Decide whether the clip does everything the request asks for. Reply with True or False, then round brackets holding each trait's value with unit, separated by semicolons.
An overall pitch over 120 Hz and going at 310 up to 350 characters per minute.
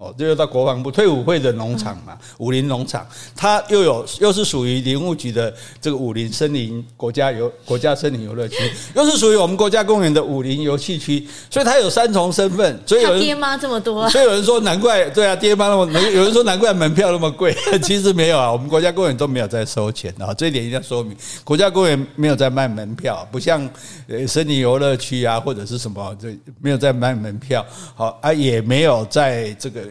True (140 Hz; 330 characters per minute)